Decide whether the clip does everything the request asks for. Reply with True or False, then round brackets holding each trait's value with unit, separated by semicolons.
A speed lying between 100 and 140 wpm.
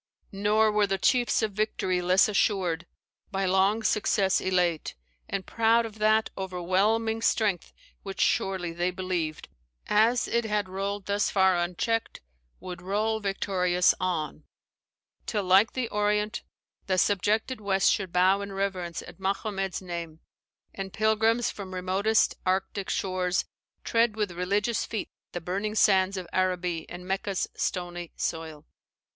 True (135 wpm)